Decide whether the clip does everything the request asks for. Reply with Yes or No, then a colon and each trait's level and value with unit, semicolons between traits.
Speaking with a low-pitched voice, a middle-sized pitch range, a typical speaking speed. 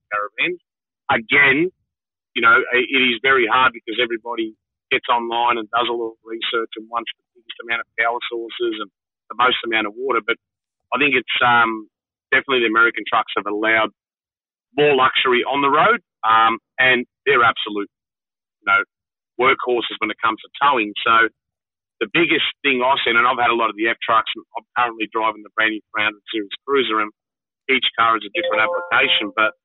No: low, 115 Hz; wide, 6.2 semitones; average, 185 wpm